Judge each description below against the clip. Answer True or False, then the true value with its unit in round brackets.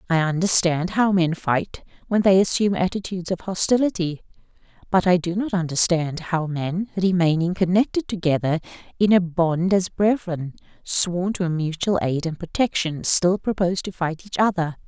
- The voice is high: False (180 Hz)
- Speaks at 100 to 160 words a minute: True (155 wpm)